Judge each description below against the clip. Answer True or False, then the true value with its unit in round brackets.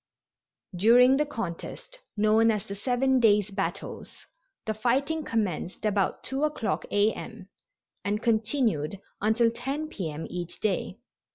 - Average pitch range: True (3.9 semitones)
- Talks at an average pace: False (130 wpm)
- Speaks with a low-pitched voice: False (220 Hz)